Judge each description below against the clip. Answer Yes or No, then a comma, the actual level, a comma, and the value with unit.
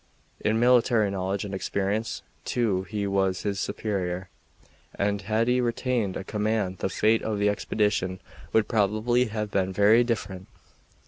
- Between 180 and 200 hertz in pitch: No, low, 105 Hz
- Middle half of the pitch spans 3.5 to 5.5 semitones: No, narrow, 2.5 semitones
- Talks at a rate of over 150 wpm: No, average, 145 wpm